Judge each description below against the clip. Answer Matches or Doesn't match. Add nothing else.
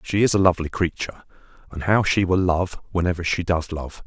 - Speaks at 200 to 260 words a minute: Matches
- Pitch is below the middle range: Matches